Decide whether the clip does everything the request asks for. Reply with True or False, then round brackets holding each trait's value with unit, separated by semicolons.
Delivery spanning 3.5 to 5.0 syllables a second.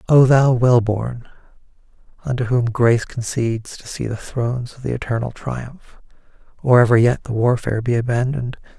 False (5.4 syllables/s)